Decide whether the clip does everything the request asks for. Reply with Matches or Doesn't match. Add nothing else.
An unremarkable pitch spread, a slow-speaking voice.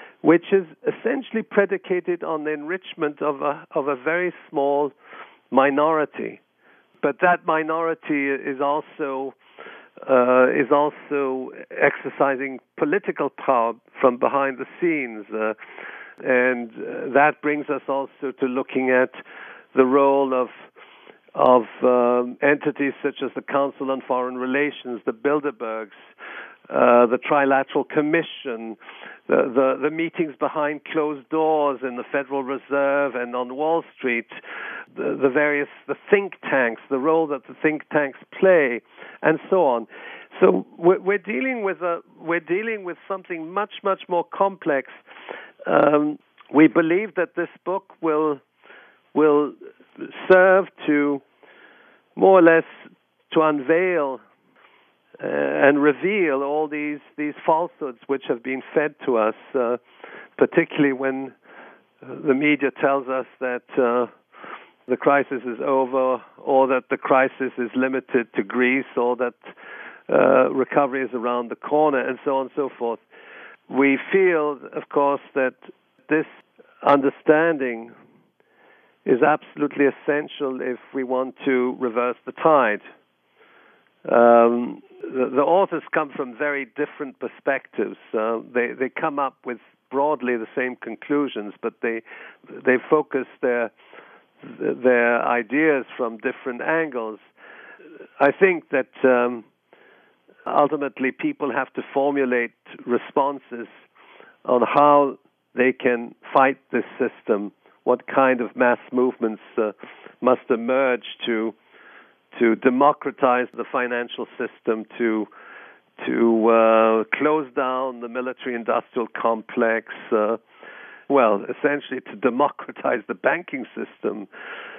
Matches